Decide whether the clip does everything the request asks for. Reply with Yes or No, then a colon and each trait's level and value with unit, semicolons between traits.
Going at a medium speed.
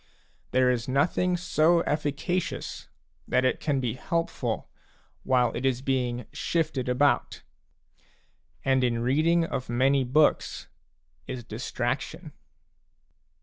No: slow, 105 wpm